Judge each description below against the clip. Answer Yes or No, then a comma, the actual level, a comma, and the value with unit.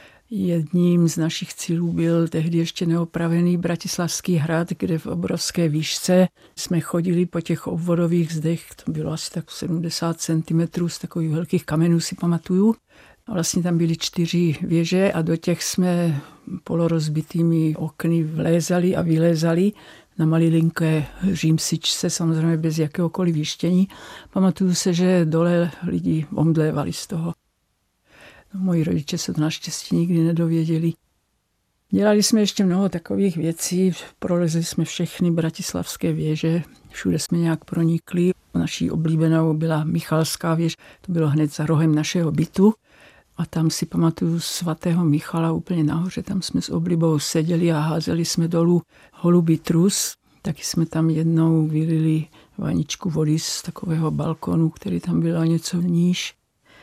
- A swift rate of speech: No, average, 140 wpm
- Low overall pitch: No, medium, 165 Hz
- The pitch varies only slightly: Yes, narrow, 1.5 semitones